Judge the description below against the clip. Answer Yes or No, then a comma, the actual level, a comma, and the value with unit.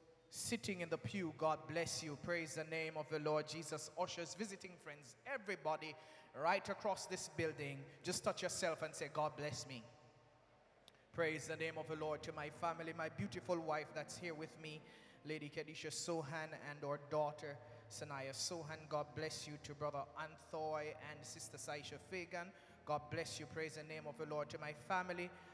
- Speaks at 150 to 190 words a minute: Yes, average, 180 wpm